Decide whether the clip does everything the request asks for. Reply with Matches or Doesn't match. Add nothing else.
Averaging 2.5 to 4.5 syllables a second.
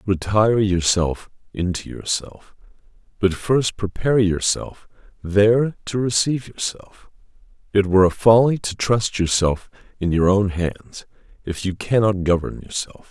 Matches